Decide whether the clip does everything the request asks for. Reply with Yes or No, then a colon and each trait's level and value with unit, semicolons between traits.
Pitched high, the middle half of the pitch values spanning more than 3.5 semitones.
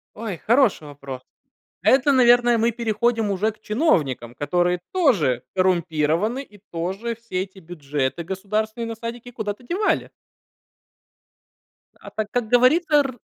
Yes: high, 215 Hz; wide, 5.5 semitones